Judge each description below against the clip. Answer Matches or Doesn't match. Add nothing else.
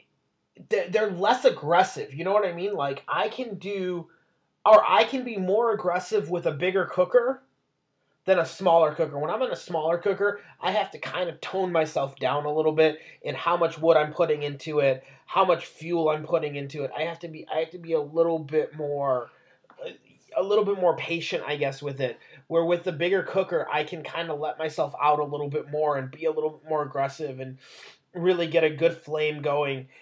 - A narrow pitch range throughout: Doesn't match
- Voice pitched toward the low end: Doesn't match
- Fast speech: Matches